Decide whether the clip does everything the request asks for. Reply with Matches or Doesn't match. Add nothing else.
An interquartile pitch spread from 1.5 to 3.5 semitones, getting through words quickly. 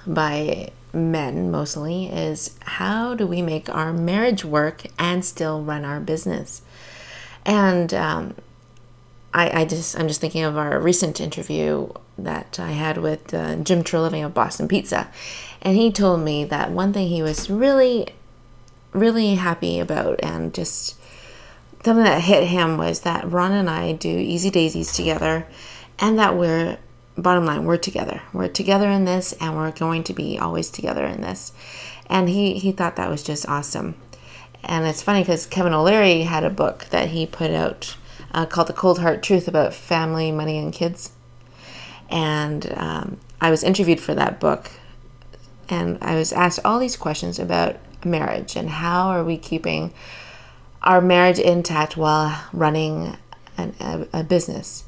Doesn't match